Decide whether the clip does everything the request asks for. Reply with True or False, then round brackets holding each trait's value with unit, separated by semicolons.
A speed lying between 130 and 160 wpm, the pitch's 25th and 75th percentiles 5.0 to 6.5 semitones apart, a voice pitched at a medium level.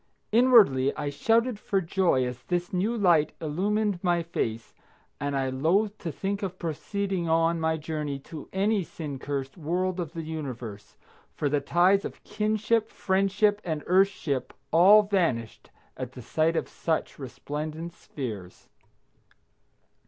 True (140 wpm; 5.5 semitones; 165 Hz)